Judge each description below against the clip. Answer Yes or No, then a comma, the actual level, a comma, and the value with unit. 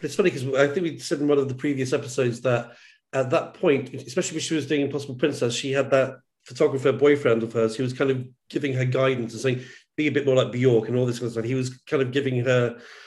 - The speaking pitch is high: No, low, 135 Hz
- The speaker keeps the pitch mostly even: Yes, narrow, 2.3 semitones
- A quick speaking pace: Yes, fast, 265 wpm